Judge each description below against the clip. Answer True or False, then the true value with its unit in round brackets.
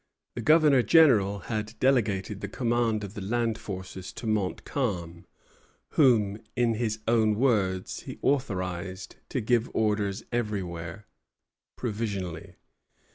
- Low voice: True (110 Hz)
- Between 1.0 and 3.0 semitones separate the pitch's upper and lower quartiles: False (3.8 semitones)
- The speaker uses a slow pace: True (115 wpm)